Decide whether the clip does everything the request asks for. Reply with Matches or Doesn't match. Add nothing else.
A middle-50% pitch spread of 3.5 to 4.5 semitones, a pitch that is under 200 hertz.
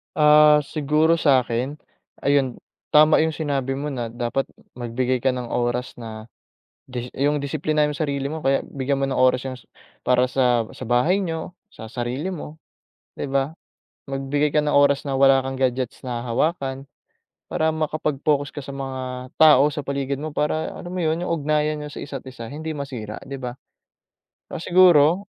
Doesn't match